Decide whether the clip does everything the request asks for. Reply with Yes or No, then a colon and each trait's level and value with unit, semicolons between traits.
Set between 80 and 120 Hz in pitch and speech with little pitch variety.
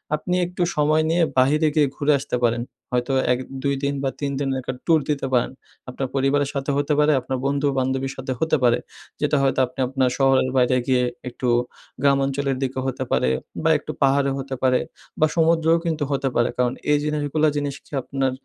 No: low, 135 Hz; narrow, 2.0 semitones